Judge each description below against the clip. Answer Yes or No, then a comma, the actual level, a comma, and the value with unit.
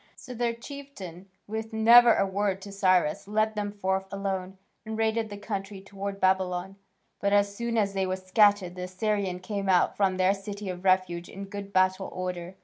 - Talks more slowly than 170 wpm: No, average, 185 wpm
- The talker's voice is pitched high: Yes, high, 195 Hz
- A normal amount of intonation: No, narrow, 2.1 semitones